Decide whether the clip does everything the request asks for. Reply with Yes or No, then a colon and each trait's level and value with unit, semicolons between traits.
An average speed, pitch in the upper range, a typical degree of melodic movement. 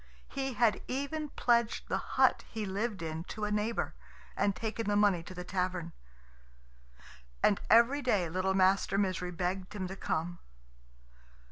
Yes: average, 150 wpm; high, 200 Hz; average, 3.7 semitones